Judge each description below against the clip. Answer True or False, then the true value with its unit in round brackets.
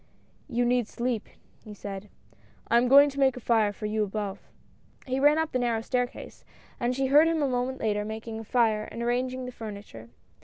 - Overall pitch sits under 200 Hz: False (240 Hz)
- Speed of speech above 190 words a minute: True (205 wpm)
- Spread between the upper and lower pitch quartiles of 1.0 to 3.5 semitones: True (3.2 semitones)